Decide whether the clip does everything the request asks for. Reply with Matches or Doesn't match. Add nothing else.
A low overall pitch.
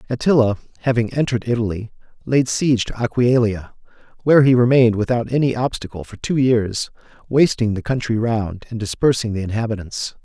Matches